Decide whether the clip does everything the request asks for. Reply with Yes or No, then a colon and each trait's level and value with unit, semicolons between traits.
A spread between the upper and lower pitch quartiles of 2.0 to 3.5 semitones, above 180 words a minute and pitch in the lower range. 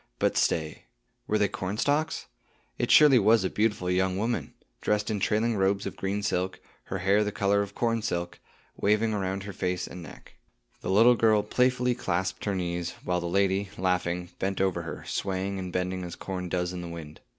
Yes: average, 2.7 semitones; average, 190 wpm; very low, 95 Hz